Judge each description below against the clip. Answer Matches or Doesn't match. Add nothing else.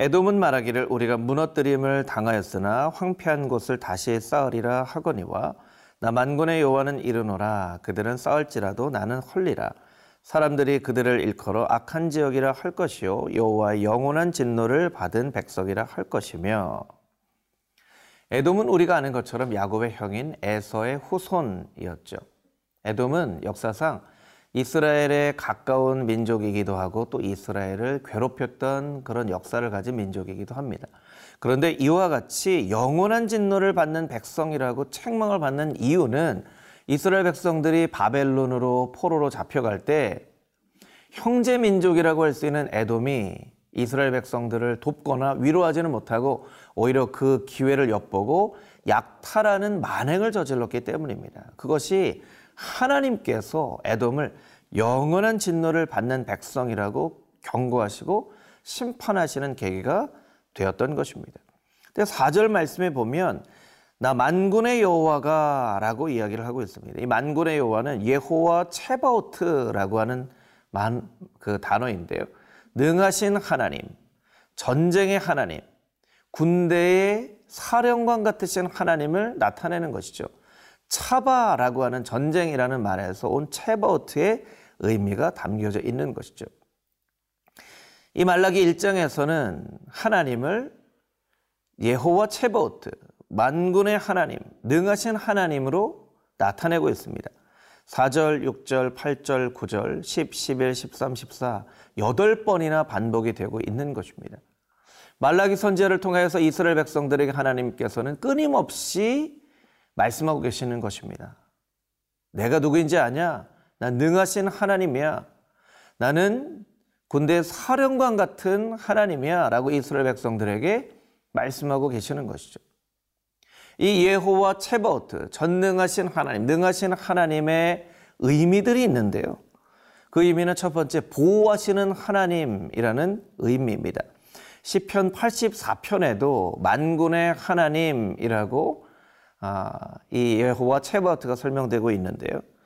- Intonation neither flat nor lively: Doesn't match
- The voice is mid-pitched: Matches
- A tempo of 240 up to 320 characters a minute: Matches